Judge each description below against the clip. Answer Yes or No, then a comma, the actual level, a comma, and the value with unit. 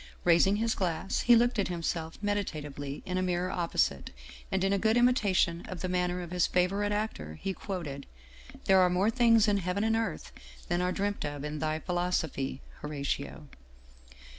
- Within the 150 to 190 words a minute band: Yes, average, 180 wpm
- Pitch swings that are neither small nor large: Yes, average, 4.0 semitones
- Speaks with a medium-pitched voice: Yes, medium, 180 Hz